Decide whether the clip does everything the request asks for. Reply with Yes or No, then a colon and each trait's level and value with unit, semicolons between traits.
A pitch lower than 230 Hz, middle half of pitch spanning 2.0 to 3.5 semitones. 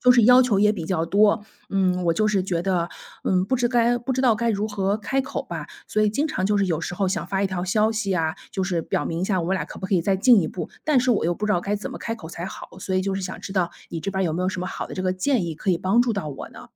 Yes: high, 195 Hz; average, 3.0 semitones